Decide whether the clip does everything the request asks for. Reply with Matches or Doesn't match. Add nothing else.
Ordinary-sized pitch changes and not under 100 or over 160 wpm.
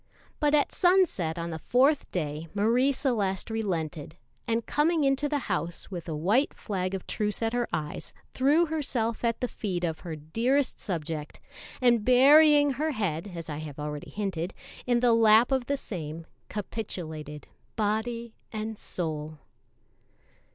Doesn't match